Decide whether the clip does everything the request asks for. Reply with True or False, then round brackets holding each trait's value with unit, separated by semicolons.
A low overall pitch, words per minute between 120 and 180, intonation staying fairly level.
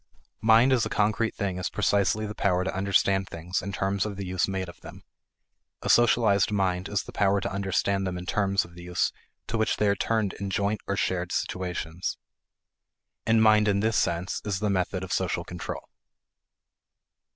False (100 Hz; 190 wpm; 2.2 semitones)